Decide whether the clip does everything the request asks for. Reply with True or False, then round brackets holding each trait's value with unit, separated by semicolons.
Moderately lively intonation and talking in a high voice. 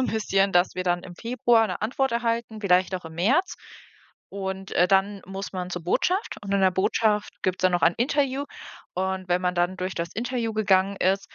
True (3.6 semitones; 195 Hz)